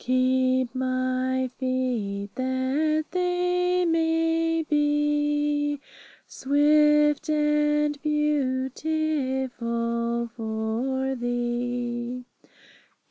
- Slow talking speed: Yes, slow, 55 wpm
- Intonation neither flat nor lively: Yes, average, 3.0 semitones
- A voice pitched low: No, very high, 265 Hz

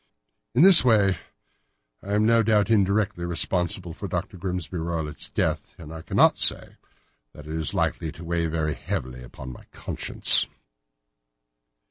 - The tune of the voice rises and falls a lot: No, average, 4.2 semitones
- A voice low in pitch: Yes, very low, 85 Hz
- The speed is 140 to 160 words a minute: Yes, average, 145 wpm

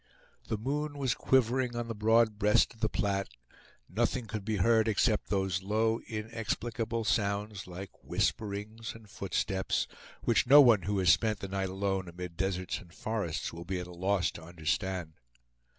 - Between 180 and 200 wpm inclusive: No, average, 165 wpm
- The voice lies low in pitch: Yes, low, 105 Hz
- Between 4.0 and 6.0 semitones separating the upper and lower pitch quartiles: No, average, 3.0 semitones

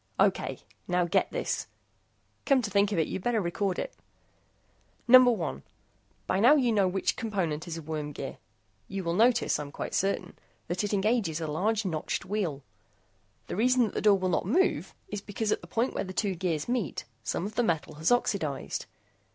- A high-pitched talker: Yes, high, 195 Hz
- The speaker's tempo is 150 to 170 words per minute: No, average, 190 wpm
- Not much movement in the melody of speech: No, average, 4.9 semitones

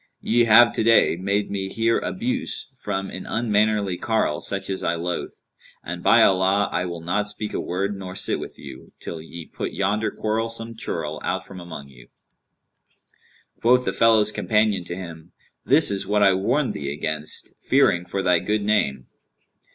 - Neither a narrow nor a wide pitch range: Yes, average, 4.0 semitones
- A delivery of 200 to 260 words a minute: No, average, 170 wpm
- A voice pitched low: Yes, low, 100 Hz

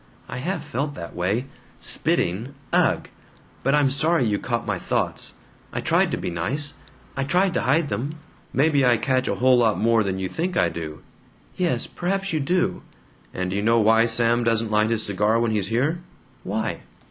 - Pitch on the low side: Yes, low, 120 Hz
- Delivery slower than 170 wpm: No, average, 190 wpm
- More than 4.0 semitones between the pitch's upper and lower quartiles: Yes, average, 5.3 semitones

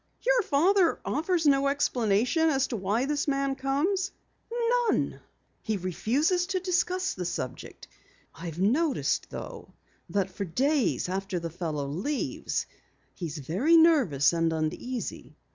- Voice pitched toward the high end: Yes, very high, 265 Hz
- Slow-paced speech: Yes, slow, 125 wpm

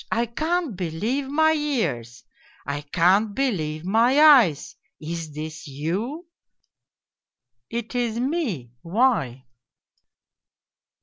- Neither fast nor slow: No, slow, 110 wpm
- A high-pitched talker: Yes, high, 205 Hz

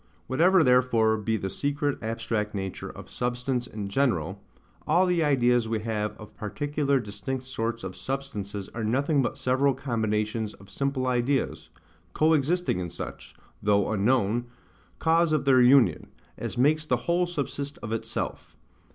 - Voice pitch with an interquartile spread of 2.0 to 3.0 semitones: No, average, 4.7 semitones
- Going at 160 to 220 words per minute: No, average, 150 wpm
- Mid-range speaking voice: No, low, 125 Hz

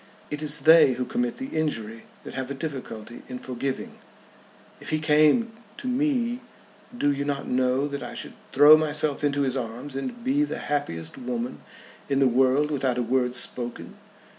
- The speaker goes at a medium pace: Yes, average, 175 wpm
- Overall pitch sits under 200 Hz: Yes, medium, 140 Hz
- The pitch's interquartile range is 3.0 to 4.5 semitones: Yes, average, 3.5 semitones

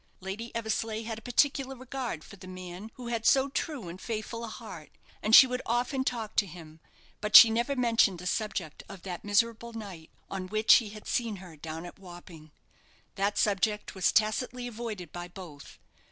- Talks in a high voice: Yes, high, 215 Hz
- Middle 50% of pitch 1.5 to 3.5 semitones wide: No, average, 4.3 semitones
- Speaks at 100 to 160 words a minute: No, average, 185 wpm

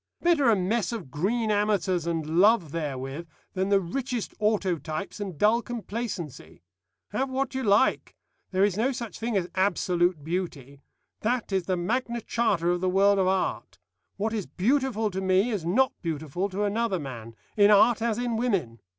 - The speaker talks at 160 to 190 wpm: Yes, average, 170 wpm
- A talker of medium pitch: No, high, 200 Hz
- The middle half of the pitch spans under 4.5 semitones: No, average, 4.8 semitones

